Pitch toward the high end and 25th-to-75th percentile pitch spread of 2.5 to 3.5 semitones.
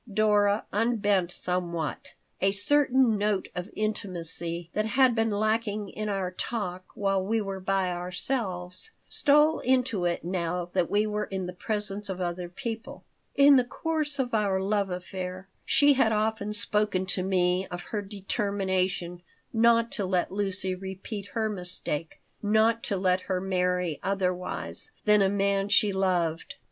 Yes: high, 195 Hz; average, 2.9 semitones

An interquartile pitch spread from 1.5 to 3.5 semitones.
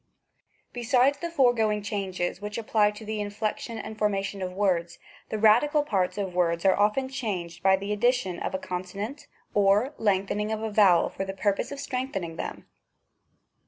Yes: average, 2.9 semitones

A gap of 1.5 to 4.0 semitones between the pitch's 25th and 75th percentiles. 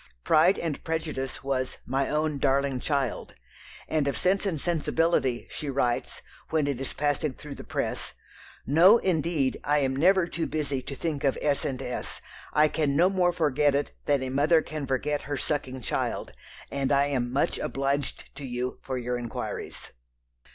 Yes: average, 2.8 semitones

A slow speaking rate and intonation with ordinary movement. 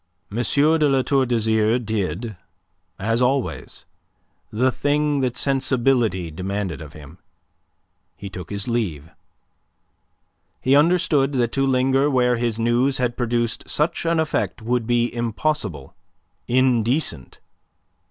Yes: slow, 115 wpm; average, 3.8 semitones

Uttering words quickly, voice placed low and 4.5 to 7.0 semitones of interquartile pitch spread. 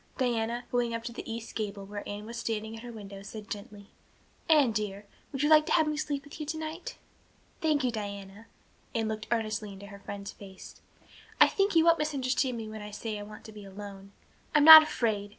No: fast, 210 wpm; high, 225 Hz; average, 5.1 semitones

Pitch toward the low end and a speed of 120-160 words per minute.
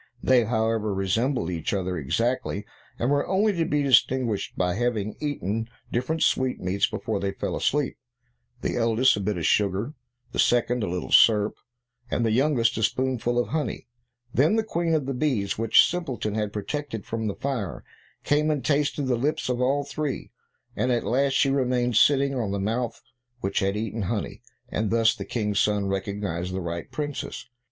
No: low, 115 Hz; average, 180 wpm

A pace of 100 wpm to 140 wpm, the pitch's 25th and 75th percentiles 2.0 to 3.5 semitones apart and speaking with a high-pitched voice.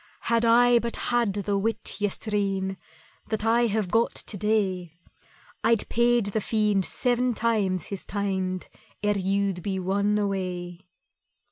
Yes: slow, 135 wpm; average, 3.0 semitones; high, 205 Hz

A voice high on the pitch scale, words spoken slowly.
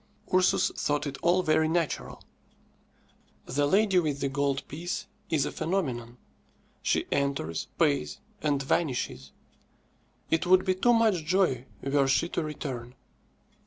No: medium, 150 Hz; slow, 130 wpm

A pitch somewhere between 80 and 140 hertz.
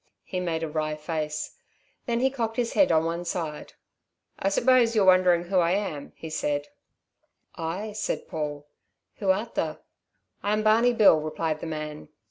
No: medium, 175 Hz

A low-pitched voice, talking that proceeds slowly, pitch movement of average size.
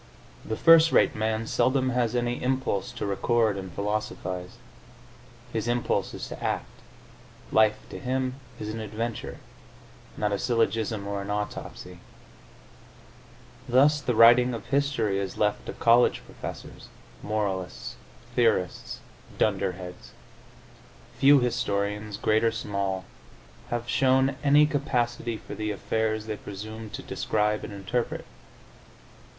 Yes: low, 110 Hz; slow, 125 wpm; average, 3.0 semitones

